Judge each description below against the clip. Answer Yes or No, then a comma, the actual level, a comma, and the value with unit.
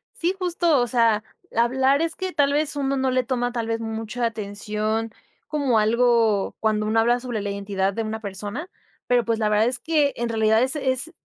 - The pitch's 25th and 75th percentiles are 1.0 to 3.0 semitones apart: No, average, 3.5 semitones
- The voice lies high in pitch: Yes, high, 235 Hz